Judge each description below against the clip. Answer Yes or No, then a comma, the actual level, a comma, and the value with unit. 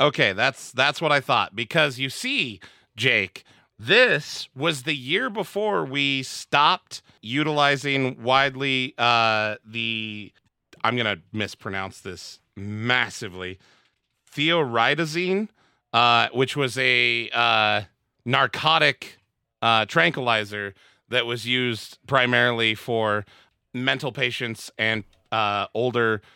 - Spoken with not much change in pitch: No, average, 3.8 semitones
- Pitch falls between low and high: No, low, 120 Hz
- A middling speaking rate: No, slow, 100 wpm